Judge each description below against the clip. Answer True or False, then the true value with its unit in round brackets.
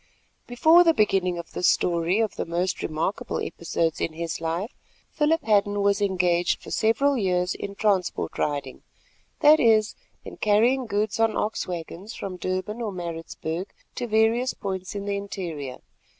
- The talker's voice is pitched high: True (200 Hz)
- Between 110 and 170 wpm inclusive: True (150 wpm)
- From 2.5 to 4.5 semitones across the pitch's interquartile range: True (4.1 semitones)